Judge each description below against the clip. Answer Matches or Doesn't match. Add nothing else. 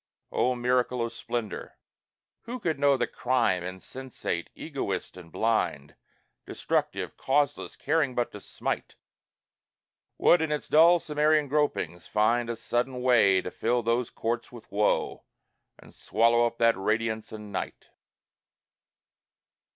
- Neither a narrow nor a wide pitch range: Matches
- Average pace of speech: Doesn't match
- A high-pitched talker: Doesn't match